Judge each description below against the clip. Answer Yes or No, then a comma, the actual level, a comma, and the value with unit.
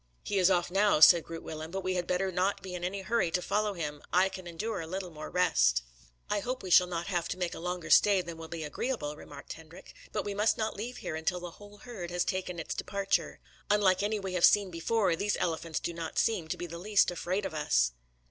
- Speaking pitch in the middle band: Yes, medium, 180 Hz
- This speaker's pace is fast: Yes, fast, 245 wpm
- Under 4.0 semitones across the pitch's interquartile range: Yes, average, 3.2 semitones